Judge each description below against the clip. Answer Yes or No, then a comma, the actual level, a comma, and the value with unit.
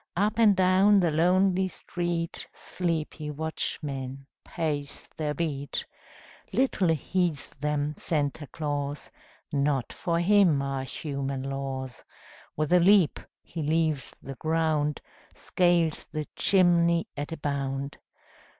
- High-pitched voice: No, medium, 155 Hz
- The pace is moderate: No, slow, 115 wpm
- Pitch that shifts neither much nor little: Yes, average, 3.6 semitones